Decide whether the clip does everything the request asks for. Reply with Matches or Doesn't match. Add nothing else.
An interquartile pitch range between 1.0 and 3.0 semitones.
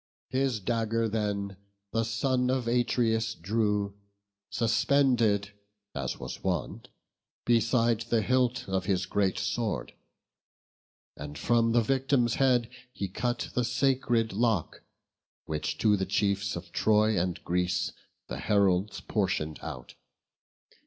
Doesn't match